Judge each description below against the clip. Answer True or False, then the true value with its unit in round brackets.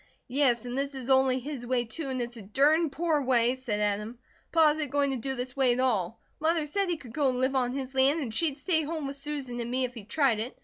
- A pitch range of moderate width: True (3.2 semitones)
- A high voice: True (265 Hz)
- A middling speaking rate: False (265 wpm)